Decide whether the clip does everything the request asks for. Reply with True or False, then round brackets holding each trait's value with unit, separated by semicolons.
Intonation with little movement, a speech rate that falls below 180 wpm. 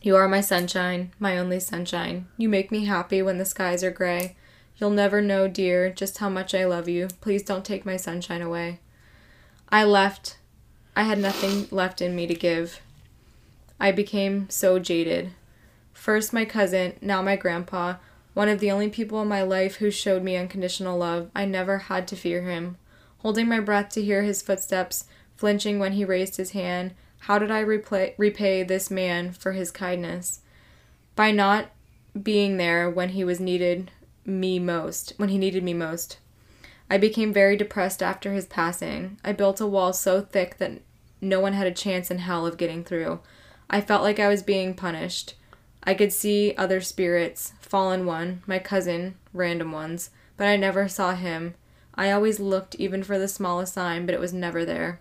False (2.0 semitones; 185 wpm)